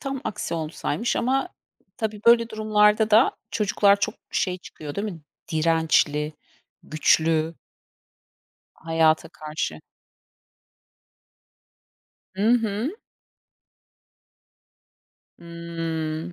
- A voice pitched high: No, medium, 175 Hz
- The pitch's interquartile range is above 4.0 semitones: Yes, average, 5.2 semitones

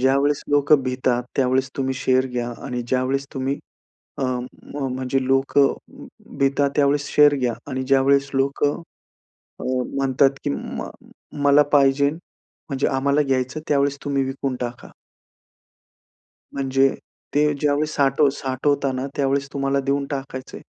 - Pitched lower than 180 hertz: Yes, low, 135 Hz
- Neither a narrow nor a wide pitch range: No, narrow, 1.3 semitones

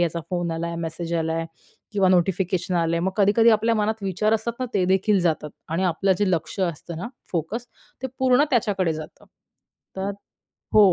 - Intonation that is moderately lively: Yes, average, 3.9 semitones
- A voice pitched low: No, medium, 185 Hz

